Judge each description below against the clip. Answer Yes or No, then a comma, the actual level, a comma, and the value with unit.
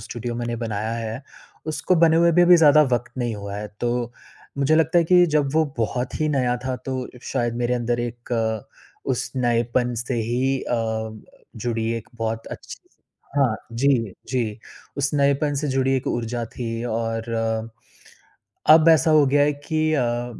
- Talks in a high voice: No, low, 120 Hz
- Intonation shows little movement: No, average, 3.6 semitones